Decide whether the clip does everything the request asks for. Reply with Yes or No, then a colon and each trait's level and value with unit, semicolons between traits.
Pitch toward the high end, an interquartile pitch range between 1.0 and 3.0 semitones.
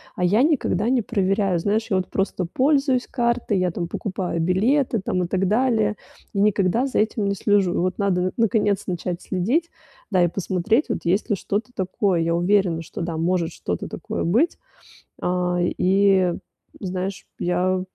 No: high, 195 Hz; average, 3.4 semitones